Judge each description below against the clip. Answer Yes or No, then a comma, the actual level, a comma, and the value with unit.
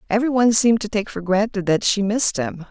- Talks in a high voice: Yes, high, 205 Hz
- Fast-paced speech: Yes, fast, 245 wpm